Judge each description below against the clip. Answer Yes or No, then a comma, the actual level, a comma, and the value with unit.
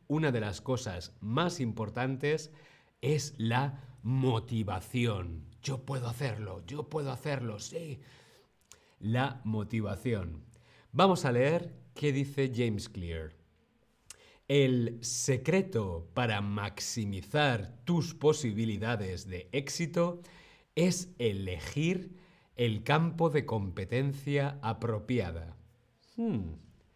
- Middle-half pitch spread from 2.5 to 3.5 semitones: No, average, 5.2 semitones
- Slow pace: Yes, slow, 90 wpm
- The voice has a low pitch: Yes, low, 120 Hz